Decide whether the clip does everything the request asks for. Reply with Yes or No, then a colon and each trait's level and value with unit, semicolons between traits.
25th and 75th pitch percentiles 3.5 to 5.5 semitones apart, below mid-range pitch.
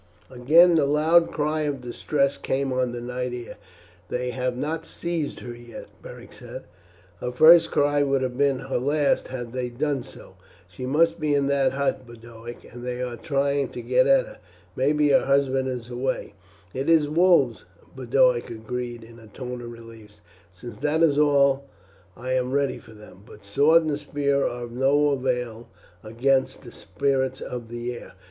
No: average, 3.0 semitones; low, 130 Hz